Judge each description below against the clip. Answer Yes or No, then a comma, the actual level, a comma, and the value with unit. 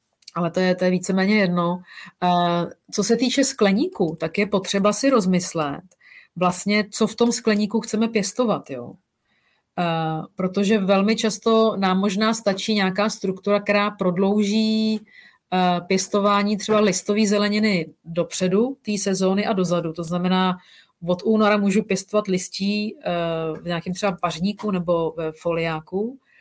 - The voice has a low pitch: No, high, 195 Hz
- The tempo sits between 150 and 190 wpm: No, average, 125 wpm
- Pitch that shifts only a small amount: No, average, 3.0 semitones